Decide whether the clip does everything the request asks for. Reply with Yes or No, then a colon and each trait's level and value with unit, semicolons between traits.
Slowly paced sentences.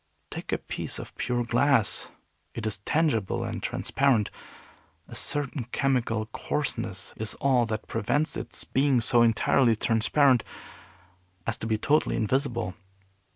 Yes: slow, 130 wpm